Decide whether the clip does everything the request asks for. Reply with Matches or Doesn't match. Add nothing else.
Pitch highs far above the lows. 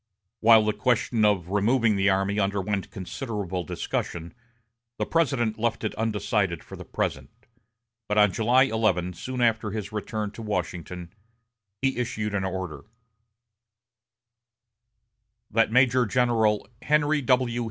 Doesn't match